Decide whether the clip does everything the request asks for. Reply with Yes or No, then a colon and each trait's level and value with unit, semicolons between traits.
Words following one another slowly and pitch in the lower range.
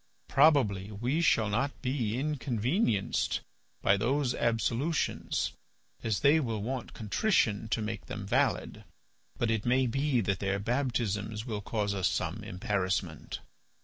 Yes: slow, 130 wpm; low, 115 Hz